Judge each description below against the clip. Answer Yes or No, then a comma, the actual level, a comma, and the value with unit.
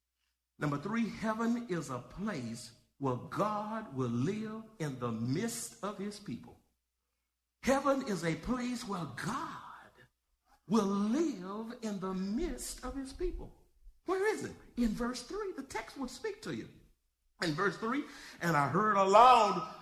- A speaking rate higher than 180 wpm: No, average, 150 wpm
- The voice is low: No, high, 205 Hz